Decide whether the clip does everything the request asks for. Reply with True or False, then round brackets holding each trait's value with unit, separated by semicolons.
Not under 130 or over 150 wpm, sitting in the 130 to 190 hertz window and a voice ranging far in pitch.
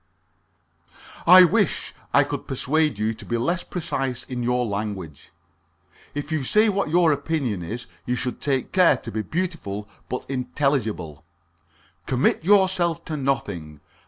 True (140 wpm; 135 Hz; 6.9 semitones)